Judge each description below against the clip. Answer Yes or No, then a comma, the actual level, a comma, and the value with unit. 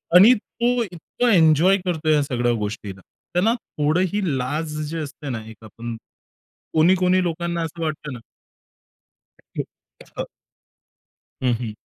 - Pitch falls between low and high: Yes, medium, 155 Hz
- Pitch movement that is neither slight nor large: No, wide, 6.2 semitones